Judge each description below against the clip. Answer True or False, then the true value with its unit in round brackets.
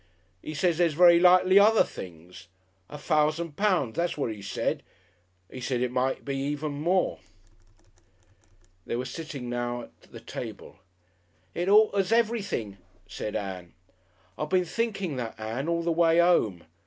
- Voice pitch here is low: False (155 Hz)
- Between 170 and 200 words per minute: False (150 wpm)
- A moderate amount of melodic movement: False (6.6 semitones)